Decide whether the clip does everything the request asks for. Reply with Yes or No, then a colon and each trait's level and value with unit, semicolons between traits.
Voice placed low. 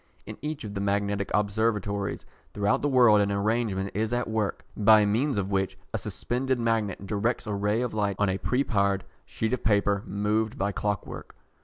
Yes: low, 105 Hz